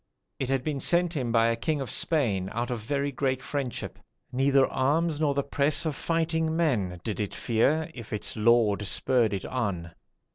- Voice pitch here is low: Yes, low, 130 Hz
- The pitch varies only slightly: No, average, 4.6 semitones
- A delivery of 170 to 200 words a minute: Yes, average, 185 wpm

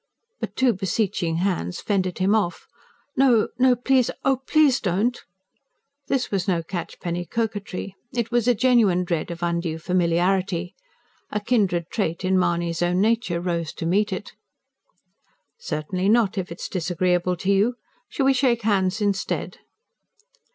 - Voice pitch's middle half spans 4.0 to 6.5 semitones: Yes, average, 4.6 semitones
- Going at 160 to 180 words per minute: No, average, 145 wpm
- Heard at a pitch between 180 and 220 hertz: Yes, high, 190 Hz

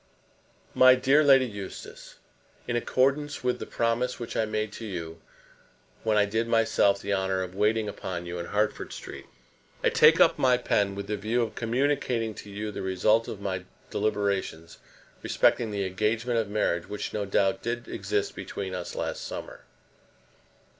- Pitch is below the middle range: Yes, low, 110 Hz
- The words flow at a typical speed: Yes, average, 165 wpm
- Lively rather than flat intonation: No, average, 3.3 semitones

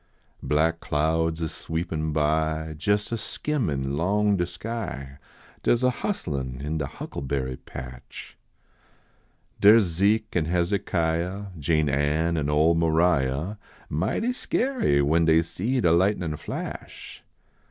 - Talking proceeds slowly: Yes, slow, 125 wpm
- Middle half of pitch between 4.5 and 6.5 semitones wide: Yes, average, 4.9 semitones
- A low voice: Yes, very low, 80 Hz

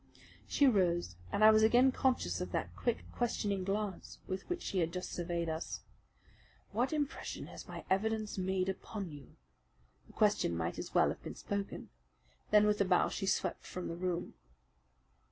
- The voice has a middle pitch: No, high, 195 Hz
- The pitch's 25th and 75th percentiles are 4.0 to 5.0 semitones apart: No, average, 3.5 semitones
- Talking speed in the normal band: Yes, average, 170 wpm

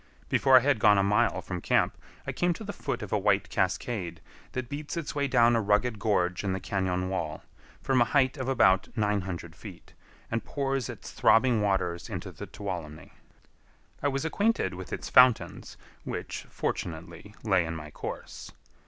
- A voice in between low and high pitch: No, low, 105 Hz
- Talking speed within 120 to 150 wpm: No, average, 180 wpm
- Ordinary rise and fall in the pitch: No, wide, 5.8 semitones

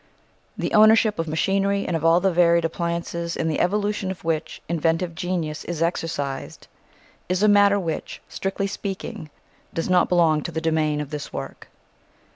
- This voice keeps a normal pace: Yes, average, 165 wpm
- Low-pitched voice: No, medium, 170 Hz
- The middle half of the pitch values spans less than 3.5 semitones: Yes, average, 3.1 semitones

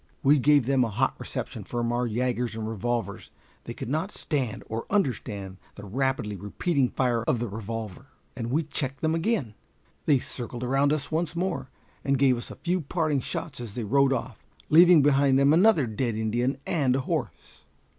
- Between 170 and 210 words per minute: Yes, average, 185 wpm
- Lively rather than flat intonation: No, average, 4.0 semitones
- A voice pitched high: No, low, 130 Hz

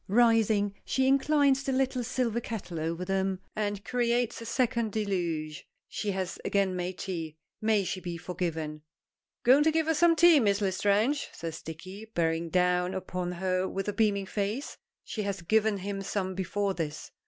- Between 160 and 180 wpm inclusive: Yes, average, 165 wpm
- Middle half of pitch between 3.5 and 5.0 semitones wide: Yes, average, 4.3 semitones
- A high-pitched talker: Yes, high, 200 Hz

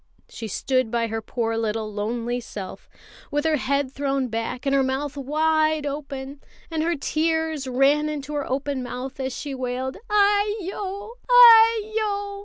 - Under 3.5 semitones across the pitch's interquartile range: No, average, 4.1 semitones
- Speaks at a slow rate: No, average, 150 wpm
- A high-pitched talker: Yes, very high, 280 Hz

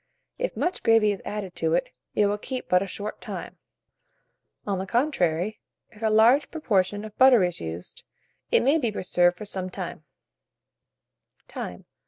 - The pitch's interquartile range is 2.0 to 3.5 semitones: No, average, 4.1 semitones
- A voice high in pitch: Yes, high, 205 Hz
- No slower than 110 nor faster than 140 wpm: No, average, 160 wpm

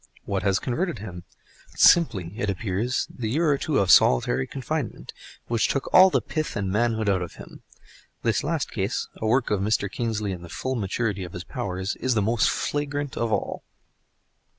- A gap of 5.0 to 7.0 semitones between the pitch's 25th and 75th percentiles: Yes, average, 5.3 semitones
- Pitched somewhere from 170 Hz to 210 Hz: No, low, 110 Hz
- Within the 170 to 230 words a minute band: Yes, average, 180 wpm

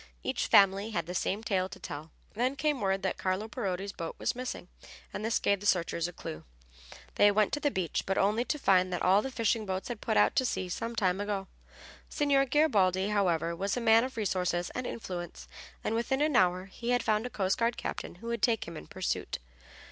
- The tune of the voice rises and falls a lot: No, average, 4.1 semitones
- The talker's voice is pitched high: Yes, high, 200 Hz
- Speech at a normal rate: No, fast, 220 wpm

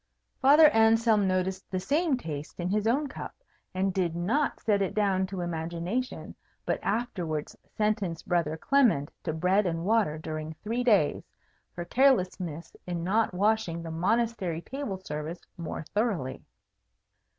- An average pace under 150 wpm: Yes, average, 140 wpm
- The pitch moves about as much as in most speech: Yes, average, 4.9 semitones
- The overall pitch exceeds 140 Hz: Yes, high, 190 Hz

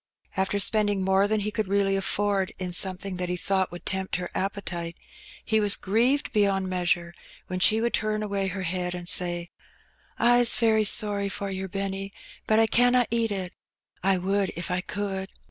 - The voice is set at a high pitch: Yes, high, 195 Hz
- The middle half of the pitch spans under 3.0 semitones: Yes, narrow, 2.4 semitones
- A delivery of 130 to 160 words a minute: No, average, 190 wpm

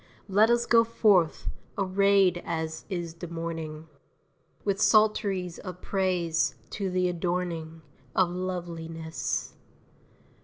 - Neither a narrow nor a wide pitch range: Yes, average, 3.0 semitones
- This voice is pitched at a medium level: Yes, medium, 180 Hz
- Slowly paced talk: Yes, slow, 105 wpm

